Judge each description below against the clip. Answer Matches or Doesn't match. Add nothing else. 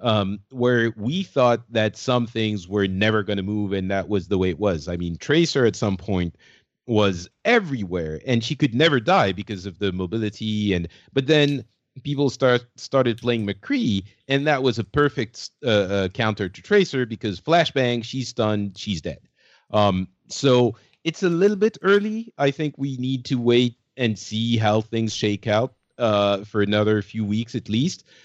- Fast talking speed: Doesn't match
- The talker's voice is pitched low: Matches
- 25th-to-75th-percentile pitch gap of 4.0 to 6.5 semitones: Matches